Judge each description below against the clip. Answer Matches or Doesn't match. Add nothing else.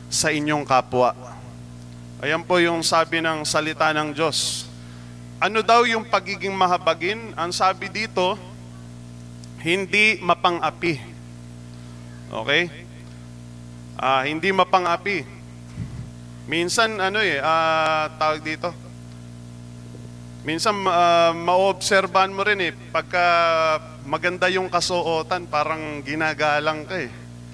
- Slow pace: Matches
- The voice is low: Doesn't match